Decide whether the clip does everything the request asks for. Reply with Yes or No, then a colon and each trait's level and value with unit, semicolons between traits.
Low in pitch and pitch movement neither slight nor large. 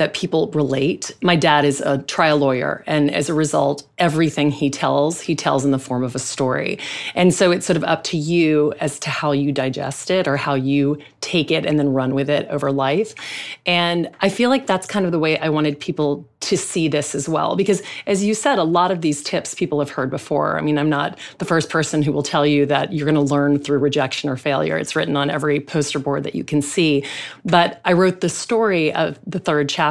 No: medium, 150 Hz; average, 3.2 semitones